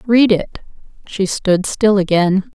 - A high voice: Yes, high, 200 Hz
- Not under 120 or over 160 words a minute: Yes, average, 140 wpm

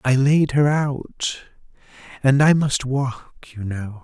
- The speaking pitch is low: Yes, low, 130 Hz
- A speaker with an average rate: Yes, average, 150 wpm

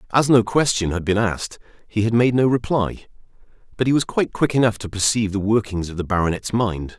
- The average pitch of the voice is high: No, low, 110 Hz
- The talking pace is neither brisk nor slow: No, fast, 215 wpm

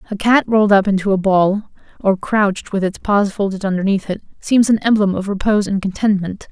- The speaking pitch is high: Yes, high, 200 Hz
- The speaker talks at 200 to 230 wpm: Yes, fast, 205 wpm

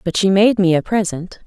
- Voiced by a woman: Yes, female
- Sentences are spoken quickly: Yes, fast, 245 wpm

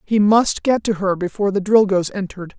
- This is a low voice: No, high, 200 Hz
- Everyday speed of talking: No, fast, 210 wpm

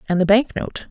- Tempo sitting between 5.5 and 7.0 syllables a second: Yes, 5.7 syllables/s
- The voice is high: Yes, high, 205 Hz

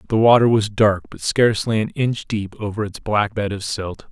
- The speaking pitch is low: Yes, low, 105 Hz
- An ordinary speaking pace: No, fast, 220 wpm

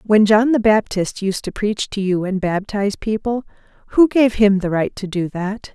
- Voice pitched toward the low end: No, high, 205 Hz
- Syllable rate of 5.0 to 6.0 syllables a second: No, 4.7 syllables/s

